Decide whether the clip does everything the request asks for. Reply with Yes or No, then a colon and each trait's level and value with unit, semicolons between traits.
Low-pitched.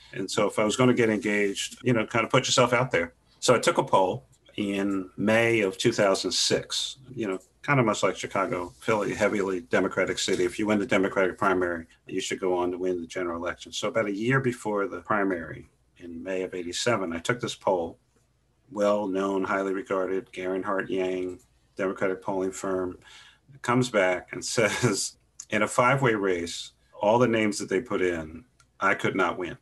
Yes: very low, 95 Hz